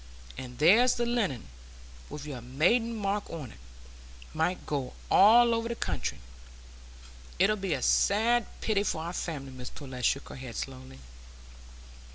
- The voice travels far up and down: Yes, wide, 8.7 semitones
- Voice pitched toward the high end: No, medium, 170 Hz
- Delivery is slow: No, average, 150 wpm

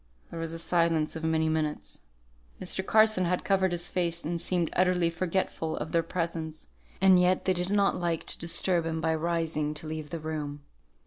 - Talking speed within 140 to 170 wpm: No, average, 190 wpm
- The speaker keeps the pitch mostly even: Yes, narrow, 2.1 semitones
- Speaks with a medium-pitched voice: Yes, medium, 165 Hz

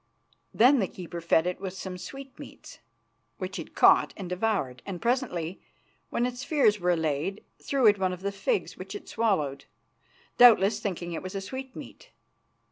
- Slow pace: No, average, 160 wpm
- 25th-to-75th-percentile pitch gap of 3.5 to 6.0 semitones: Yes, wide, 5.4 semitones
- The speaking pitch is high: Yes, high, 195 Hz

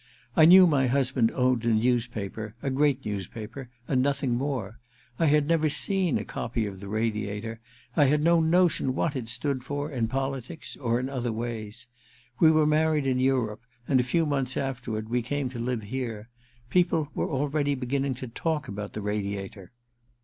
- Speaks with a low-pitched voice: Yes, low, 130 Hz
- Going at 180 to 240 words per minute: Yes, average, 185 wpm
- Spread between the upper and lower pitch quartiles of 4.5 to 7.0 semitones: No, average, 4.1 semitones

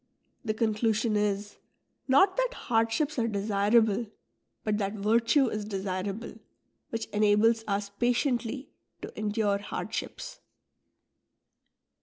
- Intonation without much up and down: Yes, narrow, 2.3 semitones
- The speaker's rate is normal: No, slow, 105 wpm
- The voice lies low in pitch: No, high, 215 Hz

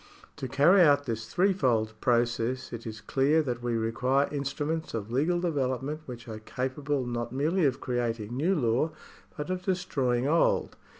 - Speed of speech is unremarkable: Yes, average, 160 wpm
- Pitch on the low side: Yes, low, 130 Hz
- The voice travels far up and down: No, average, 4.3 semitones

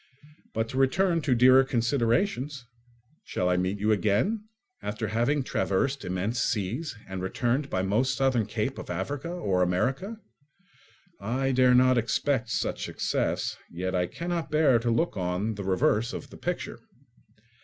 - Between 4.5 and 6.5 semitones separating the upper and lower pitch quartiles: Yes, average, 5.3 semitones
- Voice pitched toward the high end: No, low, 120 Hz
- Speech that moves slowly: No, average, 155 wpm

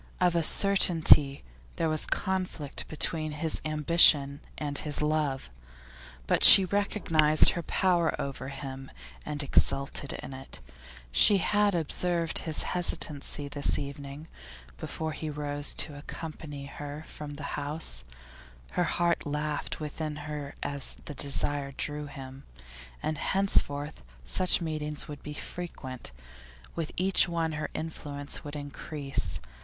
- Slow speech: Yes, slow, 130 wpm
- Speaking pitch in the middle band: Yes, medium, 150 Hz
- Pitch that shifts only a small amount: Yes, narrow, 2.3 semitones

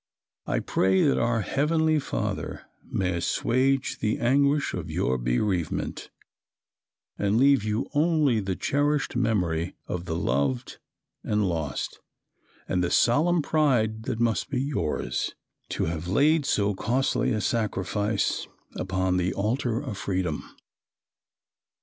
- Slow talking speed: Yes, slow, 125 wpm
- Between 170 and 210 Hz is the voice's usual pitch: No, low, 110 Hz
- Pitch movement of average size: No, wide, 6.9 semitones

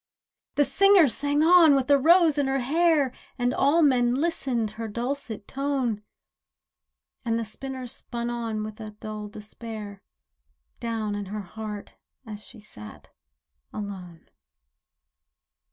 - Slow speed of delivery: Yes, slow, 130 wpm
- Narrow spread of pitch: No, average, 4.7 semitones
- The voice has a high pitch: Yes, high, 240 Hz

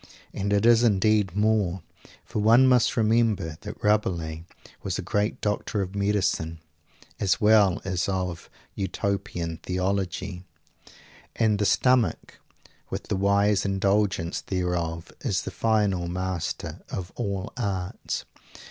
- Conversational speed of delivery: No, slow, 120 wpm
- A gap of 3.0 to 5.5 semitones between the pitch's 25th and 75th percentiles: No, narrow, 2.5 semitones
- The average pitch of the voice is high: No, low, 100 Hz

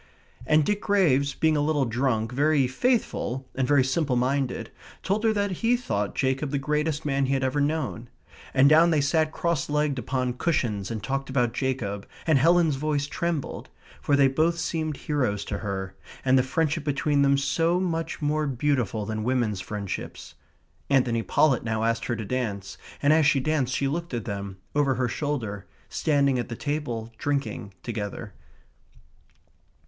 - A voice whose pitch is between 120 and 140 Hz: Yes, low, 135 Hz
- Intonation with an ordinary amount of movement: Yes, average, 4.3 semitones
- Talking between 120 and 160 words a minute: No, average, 170 wpm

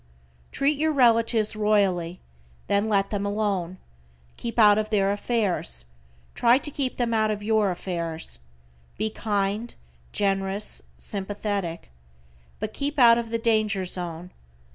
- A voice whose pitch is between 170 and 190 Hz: No, high, 210 Hz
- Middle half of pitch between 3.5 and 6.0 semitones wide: No, average, 2.9 semitones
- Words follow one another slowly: Yes, slow, 130 wpm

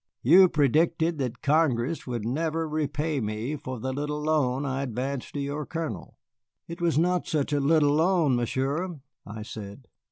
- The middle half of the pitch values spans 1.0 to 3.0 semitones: No, average, 3.8 semitones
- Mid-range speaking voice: Yes, medium, 145 Hz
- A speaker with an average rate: Yes, average, 160 wpm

